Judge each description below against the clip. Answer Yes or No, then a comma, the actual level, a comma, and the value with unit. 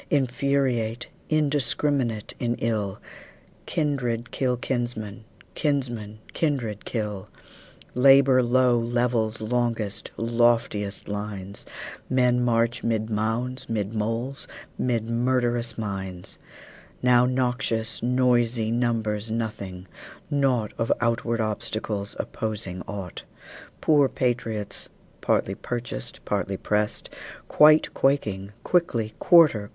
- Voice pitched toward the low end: Yes, low, 115 Hz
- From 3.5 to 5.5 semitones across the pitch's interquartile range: No, average, 2.7 semitones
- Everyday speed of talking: No, slow, 95 wpm